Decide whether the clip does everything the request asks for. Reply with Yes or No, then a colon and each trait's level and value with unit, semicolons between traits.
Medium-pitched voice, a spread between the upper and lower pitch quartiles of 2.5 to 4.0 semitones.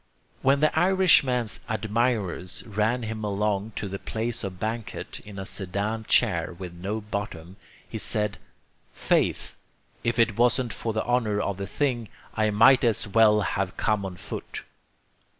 No: low, 110 Hz; average, 2.8 semitones